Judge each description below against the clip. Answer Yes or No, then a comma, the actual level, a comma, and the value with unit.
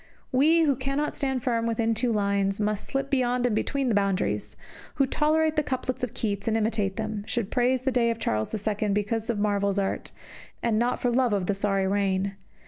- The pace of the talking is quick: Yes, fast, 210 wpm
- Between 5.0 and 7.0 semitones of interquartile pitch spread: No, average, 4.0 semitones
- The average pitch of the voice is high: Yes, high, 225 Hz